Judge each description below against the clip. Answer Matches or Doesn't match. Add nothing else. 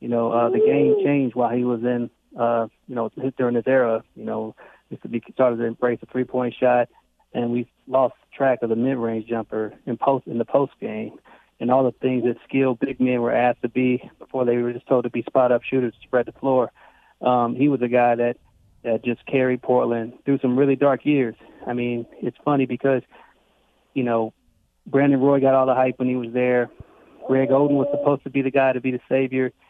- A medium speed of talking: Doesn't match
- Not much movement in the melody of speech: Matches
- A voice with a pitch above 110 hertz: Matches